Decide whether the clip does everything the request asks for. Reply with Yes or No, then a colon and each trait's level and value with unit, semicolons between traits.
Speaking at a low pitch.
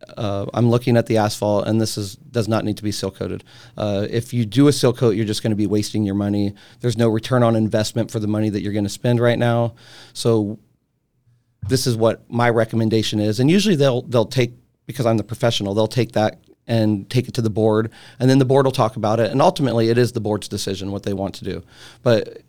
Yes: low, 115 Hz